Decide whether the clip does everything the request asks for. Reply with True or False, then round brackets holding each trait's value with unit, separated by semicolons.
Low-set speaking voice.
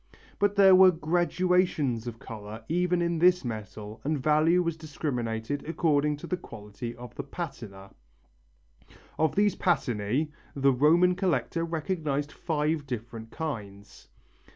False (150 Hz)